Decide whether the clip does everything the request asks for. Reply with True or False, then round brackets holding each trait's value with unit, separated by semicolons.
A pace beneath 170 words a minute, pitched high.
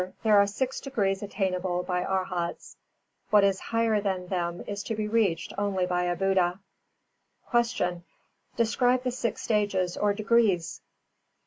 True (145 wpm; 195 Hz)